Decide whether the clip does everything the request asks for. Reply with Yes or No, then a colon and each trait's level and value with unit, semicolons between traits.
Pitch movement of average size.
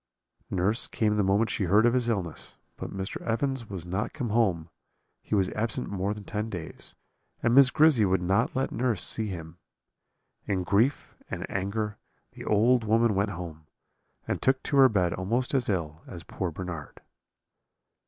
Yes: average, 4.1 semitones